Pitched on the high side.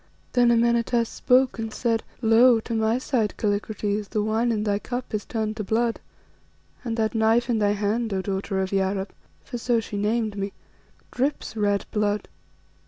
Yes: high, 220 Hz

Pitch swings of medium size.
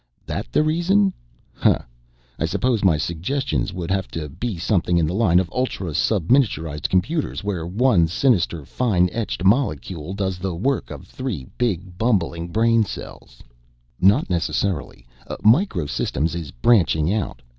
No: wide, 5.9 semitones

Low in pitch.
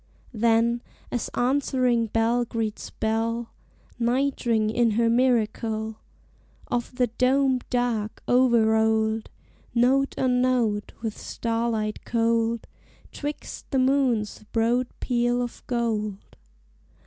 No: high, 235 Hz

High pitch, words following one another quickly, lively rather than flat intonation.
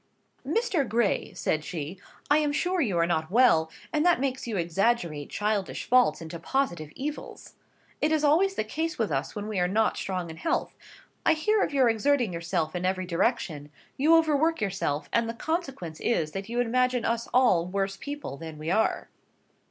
No: high, 220 Hz; average, 185 wpm; wide, 8.7 semitones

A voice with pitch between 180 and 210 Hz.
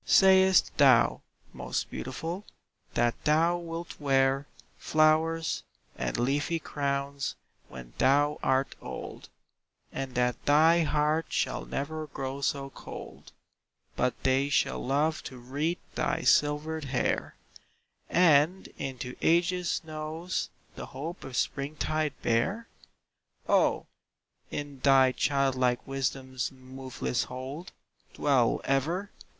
No: medium, 140 Hz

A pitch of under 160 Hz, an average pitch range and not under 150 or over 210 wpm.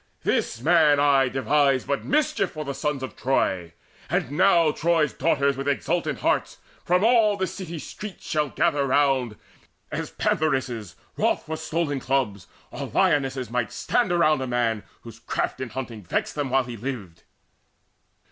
Yes: medium, 140 Hz; average, 4.1 semitones; average, 155 wpm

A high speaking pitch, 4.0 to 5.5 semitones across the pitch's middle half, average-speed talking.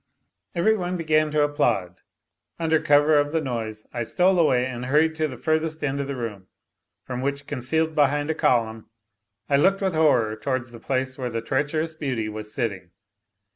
No: medium, 140 Hz; average, 4.7 semitones; average, 180 wpm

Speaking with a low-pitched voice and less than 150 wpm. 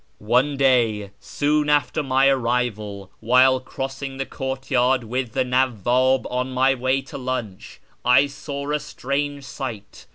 Yes: low, 130 Hz; slow, 135 wpm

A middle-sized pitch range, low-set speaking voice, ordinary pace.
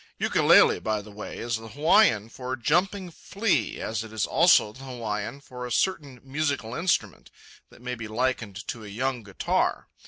Yes: average, 4.6 semitones; low, 125 Hz; average, 175 wpm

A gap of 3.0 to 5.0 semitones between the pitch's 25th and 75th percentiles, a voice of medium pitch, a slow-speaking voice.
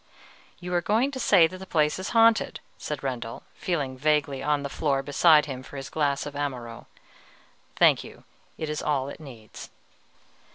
No: average, 3.8 semitones; medium, 150 Hz; average, 175 wpm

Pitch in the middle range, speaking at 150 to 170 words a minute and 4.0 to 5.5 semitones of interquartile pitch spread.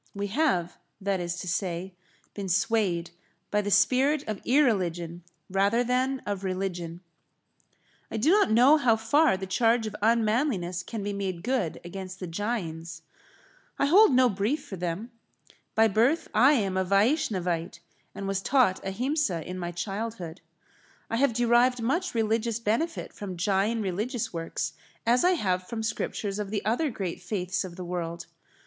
No: high, 205 Hz; average, 160 wpm; average, 4.7 semitones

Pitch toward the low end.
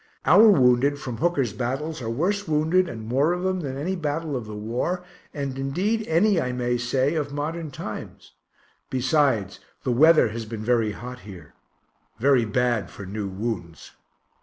Yes: low, 130 Hz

